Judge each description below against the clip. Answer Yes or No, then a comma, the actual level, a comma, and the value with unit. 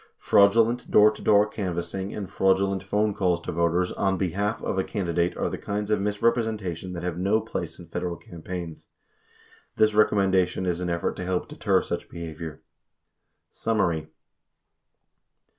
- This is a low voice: Yes, very low, 95 Hz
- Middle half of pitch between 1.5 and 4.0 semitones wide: Yes, average, 3.1 semitones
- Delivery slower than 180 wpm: Yes, average, 155 wpm